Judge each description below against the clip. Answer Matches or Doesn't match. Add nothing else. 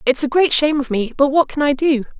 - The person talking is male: Doesn't match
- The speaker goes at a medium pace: Doesn't match